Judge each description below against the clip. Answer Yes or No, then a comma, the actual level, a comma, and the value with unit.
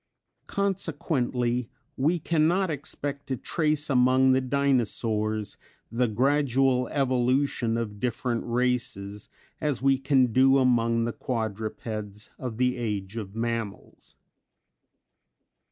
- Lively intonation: No, average, 3.1 semitones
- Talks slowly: Yes, slow, 105 wpm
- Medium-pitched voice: No, low, 125 Hz